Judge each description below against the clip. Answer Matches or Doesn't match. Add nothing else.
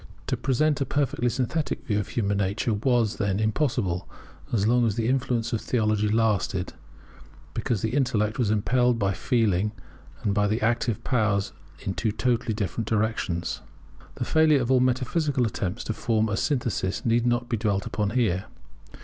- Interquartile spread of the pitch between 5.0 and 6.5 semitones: Doesn't match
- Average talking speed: Matches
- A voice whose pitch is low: Matches